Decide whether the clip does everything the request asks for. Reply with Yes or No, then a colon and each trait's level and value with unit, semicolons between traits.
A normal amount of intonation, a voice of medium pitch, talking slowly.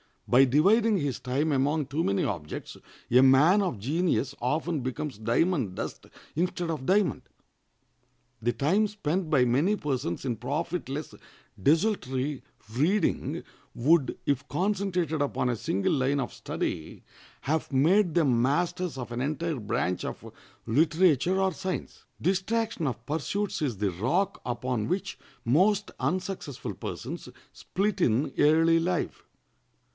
No: wide, 6.0 semitones; medium, 150 Hz; slow, 130 wpm